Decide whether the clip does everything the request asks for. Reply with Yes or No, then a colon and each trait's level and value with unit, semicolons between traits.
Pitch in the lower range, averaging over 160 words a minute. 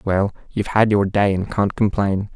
Yes: low, 100 Hz; fast, 205 wpm